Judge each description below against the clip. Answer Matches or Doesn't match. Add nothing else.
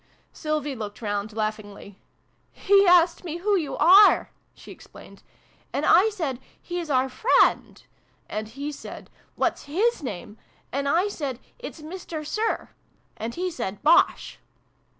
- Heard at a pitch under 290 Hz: Doesn't match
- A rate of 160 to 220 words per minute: Doesn't match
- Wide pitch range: Matches